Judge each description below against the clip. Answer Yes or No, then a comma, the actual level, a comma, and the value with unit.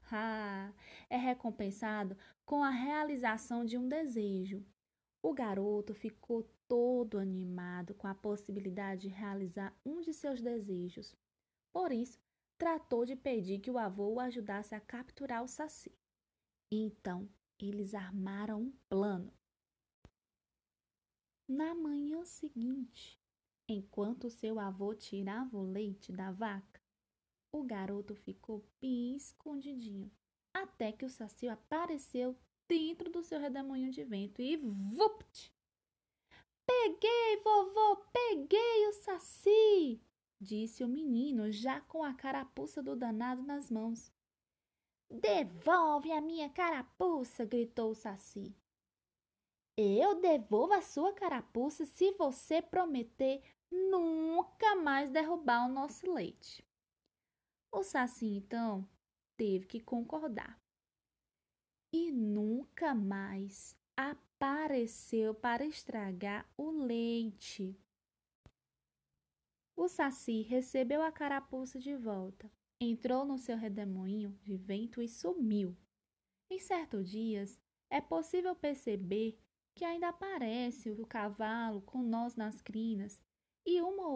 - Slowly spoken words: Yes, slow, 110 wpm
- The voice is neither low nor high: No, high, 240 Hz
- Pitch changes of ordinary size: No, wide, 6.3 semitones